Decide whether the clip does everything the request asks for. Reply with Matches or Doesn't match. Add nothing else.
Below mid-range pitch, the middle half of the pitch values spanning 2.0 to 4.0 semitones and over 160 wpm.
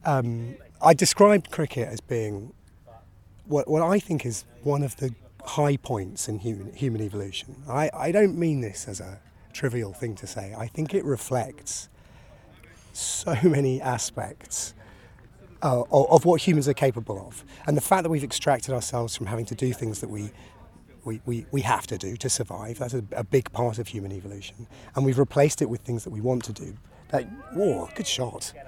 Doesn't match